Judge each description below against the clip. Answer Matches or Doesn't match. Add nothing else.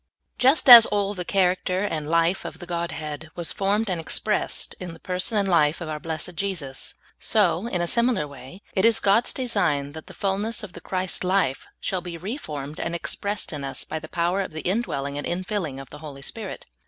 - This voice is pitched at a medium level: Matches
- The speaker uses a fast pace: Matches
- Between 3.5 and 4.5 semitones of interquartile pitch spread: Matches